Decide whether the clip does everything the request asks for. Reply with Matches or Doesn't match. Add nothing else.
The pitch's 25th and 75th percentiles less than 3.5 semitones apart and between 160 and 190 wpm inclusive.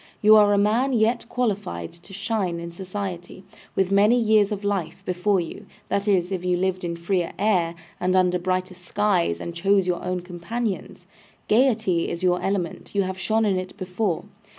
Matches